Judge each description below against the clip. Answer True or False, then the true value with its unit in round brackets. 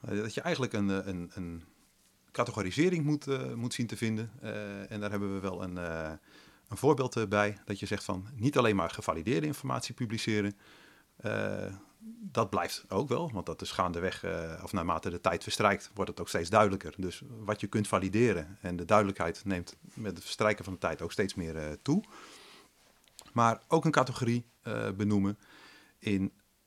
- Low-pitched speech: True (105 Hz)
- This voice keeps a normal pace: True (180 wpm)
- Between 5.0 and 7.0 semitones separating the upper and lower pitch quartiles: False (3.4 semitones)